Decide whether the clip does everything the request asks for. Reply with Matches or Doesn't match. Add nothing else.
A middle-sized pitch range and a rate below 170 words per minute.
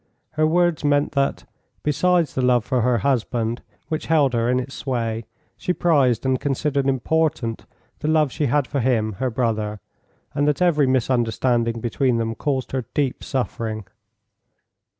Matches